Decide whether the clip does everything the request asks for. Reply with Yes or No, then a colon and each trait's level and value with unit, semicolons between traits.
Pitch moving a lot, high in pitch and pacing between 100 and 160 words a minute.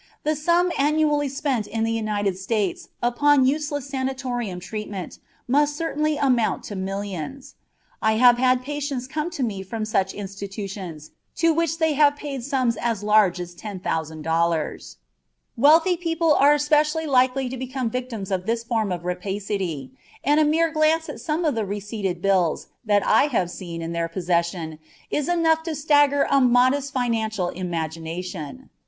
Yes: wide, 7.2 semitones; high, 240 Hz; average, 155 wpm